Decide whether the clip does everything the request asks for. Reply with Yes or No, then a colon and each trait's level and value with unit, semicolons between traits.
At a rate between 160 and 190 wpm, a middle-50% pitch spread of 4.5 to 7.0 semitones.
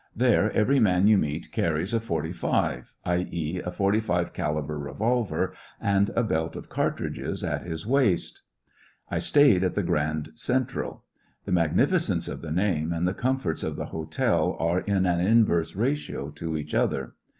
Yes: average, 170 wpm; average, 5.0 semitones